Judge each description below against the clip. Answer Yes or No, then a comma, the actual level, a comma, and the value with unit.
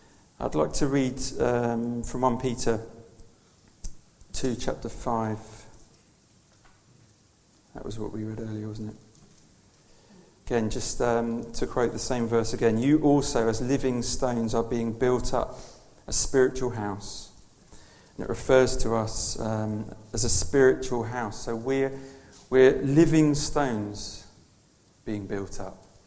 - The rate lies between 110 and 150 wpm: Yes, slow, 135 wpm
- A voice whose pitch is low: Yes, low, 115 Hz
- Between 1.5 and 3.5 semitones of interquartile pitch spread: Yes, average, 3.1 semitones